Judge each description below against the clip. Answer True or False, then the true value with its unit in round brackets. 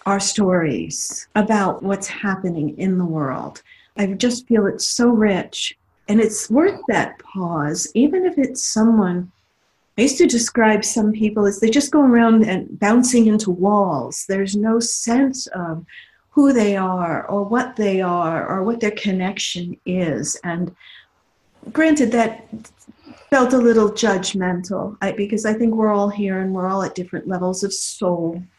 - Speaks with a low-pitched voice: False (205 Hz)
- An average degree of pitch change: True (3.7 semitones)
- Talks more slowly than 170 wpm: True (160 wpm)